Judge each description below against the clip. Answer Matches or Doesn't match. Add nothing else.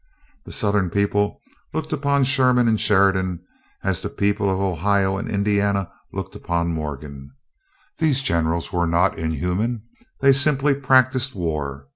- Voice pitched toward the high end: Doesn't match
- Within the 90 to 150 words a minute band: Matches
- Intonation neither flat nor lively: Doesn't match